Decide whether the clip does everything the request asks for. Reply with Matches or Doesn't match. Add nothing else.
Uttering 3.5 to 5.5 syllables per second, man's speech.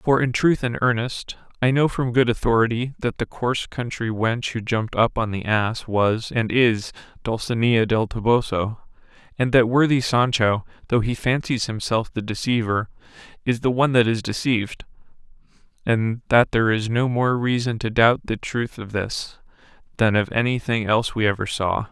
Matches